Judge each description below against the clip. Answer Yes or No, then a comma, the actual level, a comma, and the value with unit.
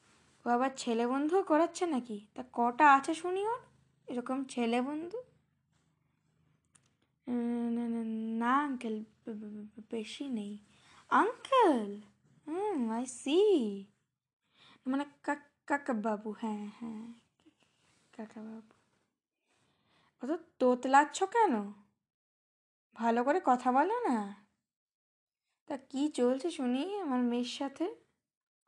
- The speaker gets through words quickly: No, average, 80 wpm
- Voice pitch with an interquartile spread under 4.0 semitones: No, average, 4.6 semitones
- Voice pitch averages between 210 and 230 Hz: No, very high, 255 Hz